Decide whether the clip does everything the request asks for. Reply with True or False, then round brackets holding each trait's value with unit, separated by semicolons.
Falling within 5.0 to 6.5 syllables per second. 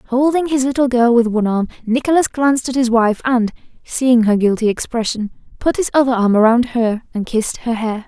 True (5.4 syllables/s)